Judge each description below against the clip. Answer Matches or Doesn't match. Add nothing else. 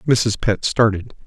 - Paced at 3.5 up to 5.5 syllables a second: Matches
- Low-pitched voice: Matches